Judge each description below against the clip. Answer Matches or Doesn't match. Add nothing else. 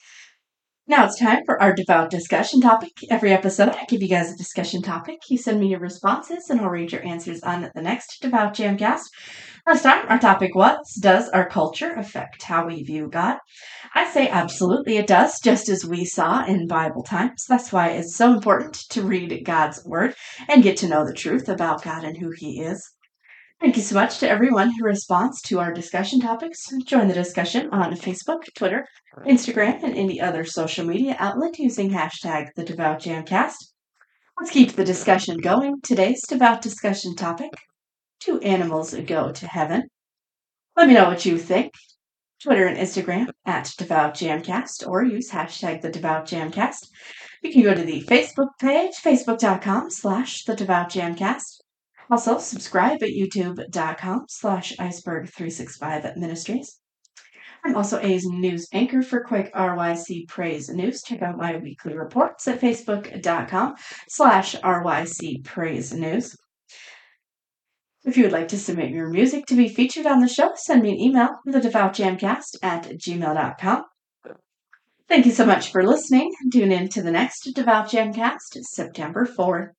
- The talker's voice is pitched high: Matches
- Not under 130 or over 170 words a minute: Matches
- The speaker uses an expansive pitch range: Matches